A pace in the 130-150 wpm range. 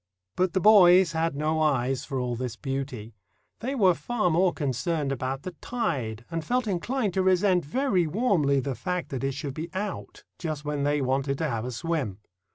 No: average, 190 wpm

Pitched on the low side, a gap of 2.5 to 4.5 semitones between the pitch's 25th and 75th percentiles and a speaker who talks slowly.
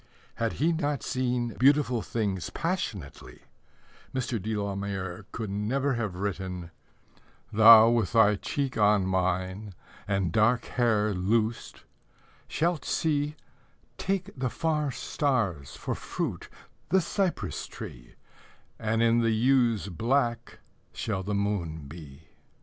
No: low, 110 Hz; average, 5.0 semitones; slow, 120 wpm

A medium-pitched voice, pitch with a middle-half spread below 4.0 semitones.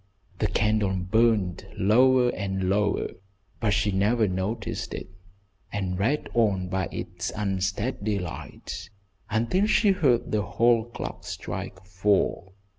No: low, 105 Hz; average, 3.5 semitones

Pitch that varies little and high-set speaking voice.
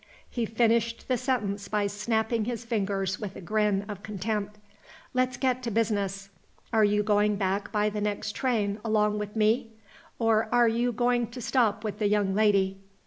Yes: narrow, 2.1 semitones; high, 215 Hz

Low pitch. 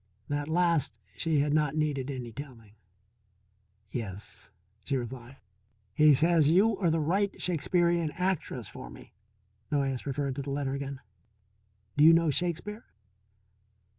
No: medium, 150 Hz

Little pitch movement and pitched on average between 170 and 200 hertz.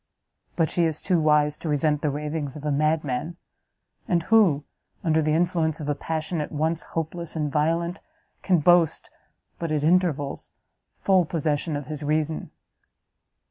No: narrow, 2.2 semitones; medium, 155 Hz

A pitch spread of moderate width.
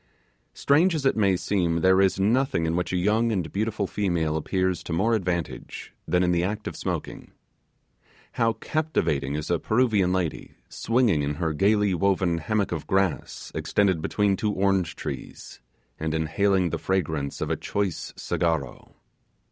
Yes: average, 3.7 semitones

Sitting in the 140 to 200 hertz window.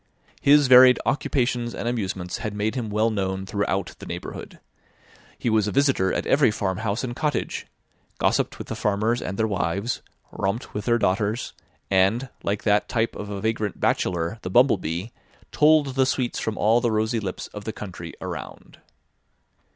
No: low, 110 Hz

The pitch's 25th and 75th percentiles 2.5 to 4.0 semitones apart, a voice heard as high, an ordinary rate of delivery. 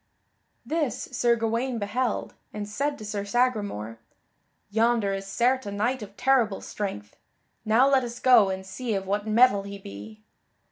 Yes: average, 3.7 semitones; high, 215 Hz; average, 155 wpm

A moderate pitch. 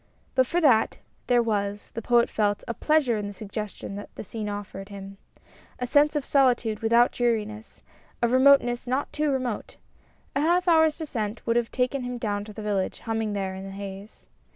No: high, 230 Hz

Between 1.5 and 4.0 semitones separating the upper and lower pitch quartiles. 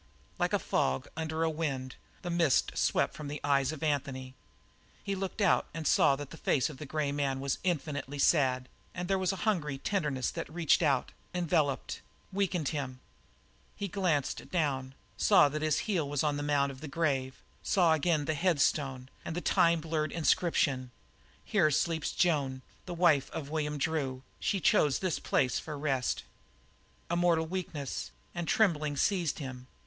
Yes: average, 3.6 semitones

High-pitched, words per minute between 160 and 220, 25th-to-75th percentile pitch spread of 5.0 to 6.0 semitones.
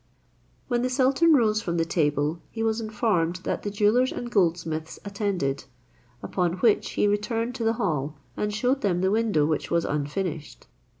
Yes: high, 200 Hz; average, 165 wpm; wide, 5.6 semitones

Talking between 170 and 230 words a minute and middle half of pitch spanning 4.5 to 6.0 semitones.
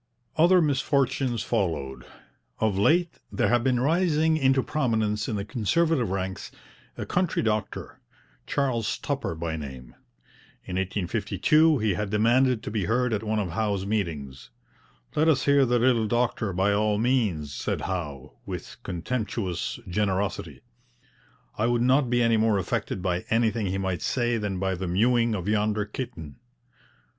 No: average, 150 wpm; average, 4.9 semitones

